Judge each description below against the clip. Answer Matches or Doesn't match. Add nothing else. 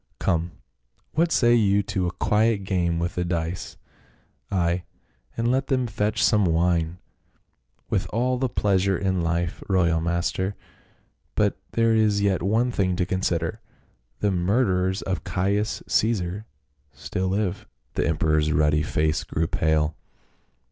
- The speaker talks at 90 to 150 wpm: Matches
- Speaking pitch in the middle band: Doesn't match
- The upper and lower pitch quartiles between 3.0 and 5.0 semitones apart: Matches